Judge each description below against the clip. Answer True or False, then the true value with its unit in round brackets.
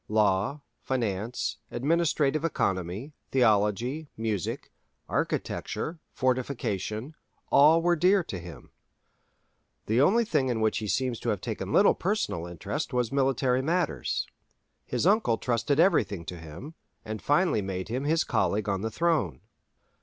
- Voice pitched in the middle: False (125 Hz)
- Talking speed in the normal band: False (130 wpm)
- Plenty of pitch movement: True (6.4 semitones)